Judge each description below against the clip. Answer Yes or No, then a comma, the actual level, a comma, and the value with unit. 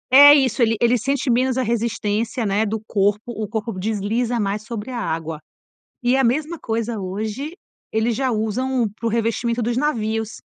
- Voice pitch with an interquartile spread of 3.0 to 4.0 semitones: No, narrow, 2.6 semitones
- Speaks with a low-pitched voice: No, high, 230 Hz